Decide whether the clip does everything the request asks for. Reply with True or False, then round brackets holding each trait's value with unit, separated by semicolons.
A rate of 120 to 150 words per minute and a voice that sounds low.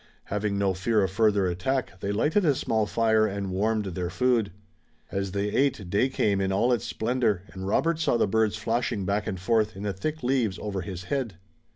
False (205 wpm; 105 Hz)